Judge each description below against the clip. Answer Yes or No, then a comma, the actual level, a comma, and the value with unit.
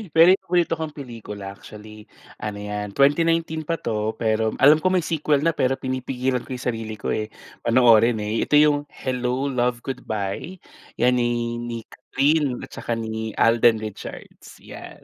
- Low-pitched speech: Yes, low, 125 Hz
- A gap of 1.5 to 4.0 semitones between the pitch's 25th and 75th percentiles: No, average, 4.8 semitones